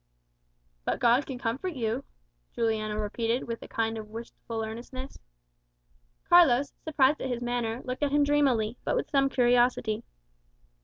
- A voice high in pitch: Yes, high, 245 Hz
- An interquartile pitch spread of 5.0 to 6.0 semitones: No, average, 3.3 semitones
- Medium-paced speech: Yes, average, 145 wpm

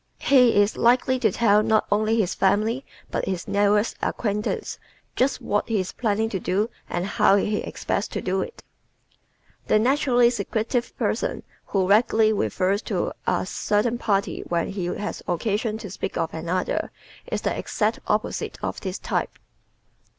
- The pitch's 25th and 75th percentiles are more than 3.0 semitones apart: No, average, 2.7 semitones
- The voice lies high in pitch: Yes, high, 210 Hz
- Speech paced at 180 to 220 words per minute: No, average, 160 wpm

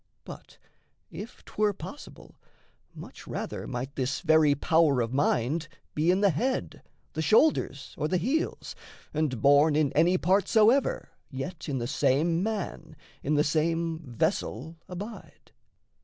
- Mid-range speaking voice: Yes, medium, 160 Hz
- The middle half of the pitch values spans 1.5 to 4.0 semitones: No, average, 4.6 semitones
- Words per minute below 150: Yes, average, 140 wpm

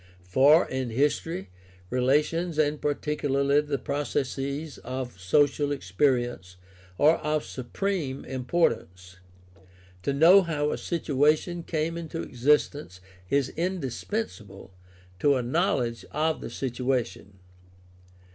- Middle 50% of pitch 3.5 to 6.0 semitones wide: Yes, average, 3.9 semitones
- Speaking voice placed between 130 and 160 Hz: Yes, medium, 140 Hz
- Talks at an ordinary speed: No, slow, 105 wpm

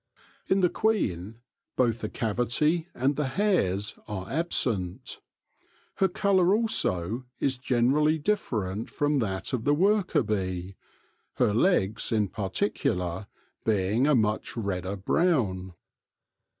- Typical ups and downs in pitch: No, wide, 8.3 semitones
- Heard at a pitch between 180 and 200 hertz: No, low, 120 Hz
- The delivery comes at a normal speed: No, slow, 115 wpm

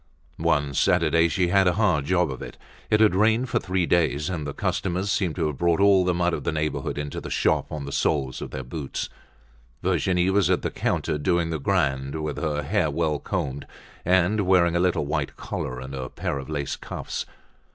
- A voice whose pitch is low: Yes, very low, 85 Hz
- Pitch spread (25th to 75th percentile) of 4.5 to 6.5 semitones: No, average, 4.1 semitones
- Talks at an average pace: No, fast, 210 wpm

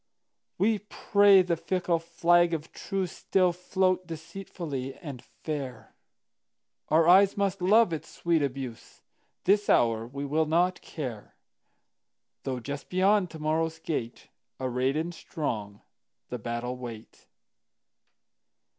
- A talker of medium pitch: Yes, medium, 160 Hz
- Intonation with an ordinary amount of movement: No, wide, 5.9 semitones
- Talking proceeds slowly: Yes, slow, 100 wpm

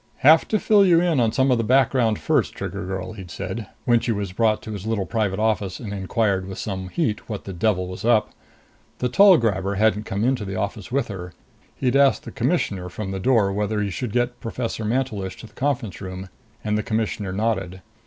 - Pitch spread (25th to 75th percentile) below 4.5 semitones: Yes, average, 4.0 semitones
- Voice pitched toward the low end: Yes, low, 110 Hz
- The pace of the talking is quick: Yes, fast, 215 wpm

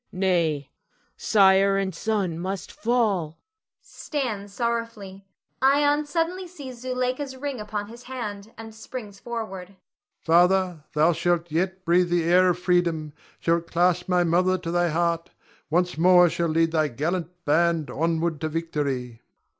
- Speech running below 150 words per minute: Yes, average, 140 wpm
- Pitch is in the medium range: Yes, medium, 180 Hz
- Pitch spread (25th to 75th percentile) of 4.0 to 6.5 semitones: Yes, average, 4.7 semitones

